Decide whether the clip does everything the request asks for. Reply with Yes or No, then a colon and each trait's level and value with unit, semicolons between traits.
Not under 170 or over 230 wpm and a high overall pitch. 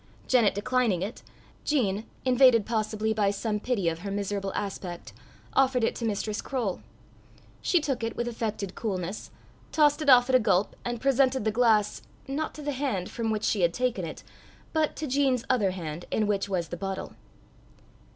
Yes: average, 180 wpm; high, 220 Hz